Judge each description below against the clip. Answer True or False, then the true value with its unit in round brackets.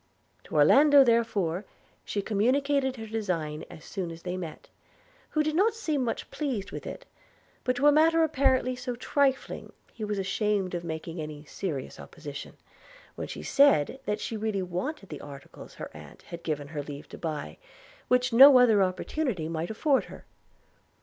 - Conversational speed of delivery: True (170 wpm)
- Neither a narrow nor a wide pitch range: False (8.1 semitones)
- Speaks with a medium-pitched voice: False (210 Hz)